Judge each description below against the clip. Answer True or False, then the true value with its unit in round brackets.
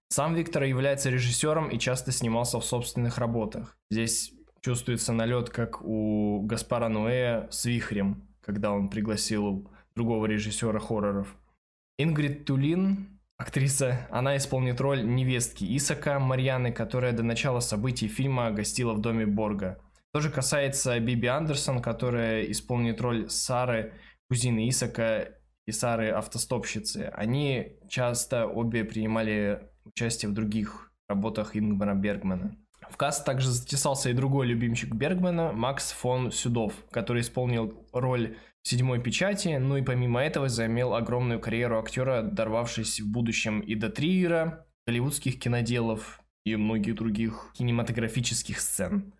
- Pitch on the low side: True (120 Hz)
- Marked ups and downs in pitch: False (3.0 semitones)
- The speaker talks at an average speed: True (125 wpm)